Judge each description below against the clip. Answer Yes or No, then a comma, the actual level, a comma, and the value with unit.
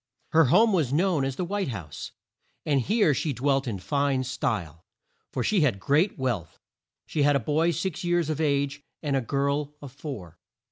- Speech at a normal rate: Yes, average, 185 wpm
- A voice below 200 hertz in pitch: Yes, medium, 140 Hz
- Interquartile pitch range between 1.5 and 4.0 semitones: Yes, average, 3.6 semitones